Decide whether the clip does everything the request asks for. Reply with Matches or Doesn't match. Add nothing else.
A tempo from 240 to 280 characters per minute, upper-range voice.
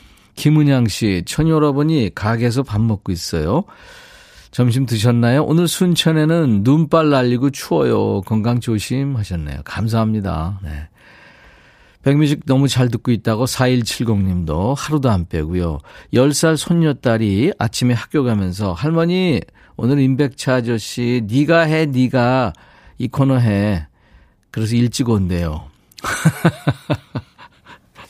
Doesn't match